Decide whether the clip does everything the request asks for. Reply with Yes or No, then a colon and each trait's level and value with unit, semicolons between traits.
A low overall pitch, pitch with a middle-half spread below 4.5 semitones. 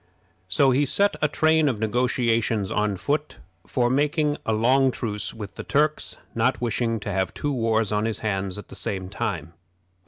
No: low, 115 Hz; average, 4.8 semitones